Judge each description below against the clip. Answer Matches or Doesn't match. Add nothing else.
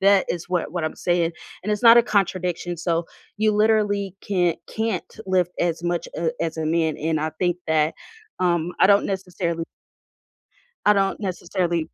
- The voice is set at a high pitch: Doesn't match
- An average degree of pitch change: Matches